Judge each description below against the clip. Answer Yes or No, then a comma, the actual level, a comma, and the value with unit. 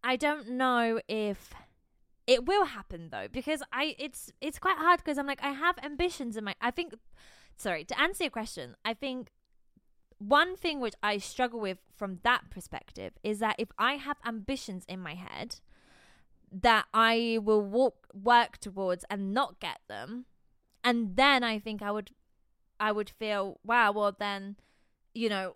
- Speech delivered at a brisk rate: No, average, 170 wpm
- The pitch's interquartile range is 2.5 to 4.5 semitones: No, average, 5.1 semitones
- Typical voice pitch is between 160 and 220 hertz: No, high, 235 Hz